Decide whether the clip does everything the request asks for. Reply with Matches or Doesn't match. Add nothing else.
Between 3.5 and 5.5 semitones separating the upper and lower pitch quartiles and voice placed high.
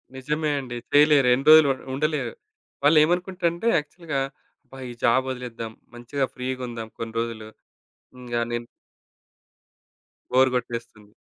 Doesn't match